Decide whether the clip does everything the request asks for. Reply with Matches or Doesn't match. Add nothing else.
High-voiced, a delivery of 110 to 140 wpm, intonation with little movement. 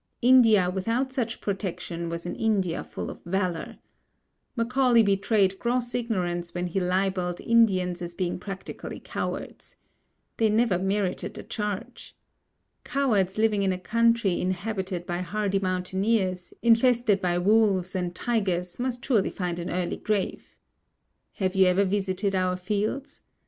Doesn't match